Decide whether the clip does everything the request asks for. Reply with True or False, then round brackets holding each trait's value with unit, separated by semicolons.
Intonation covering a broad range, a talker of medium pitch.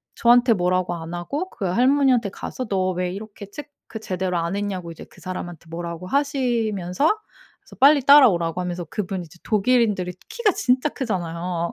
False (6.1 semitones; 195 Hz)